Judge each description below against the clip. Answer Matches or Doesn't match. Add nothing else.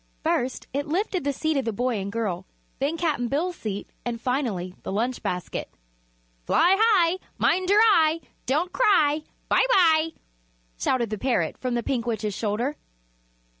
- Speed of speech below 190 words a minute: Matches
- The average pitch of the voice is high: Matches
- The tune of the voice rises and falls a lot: Matches